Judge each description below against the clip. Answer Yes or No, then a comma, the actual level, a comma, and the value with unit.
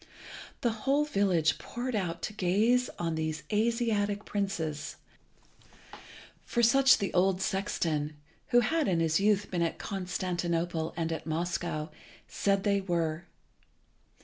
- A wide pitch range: No, average, 4.3 semitones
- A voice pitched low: No, high, 190 Hz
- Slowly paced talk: Yes, slow, 125 wpm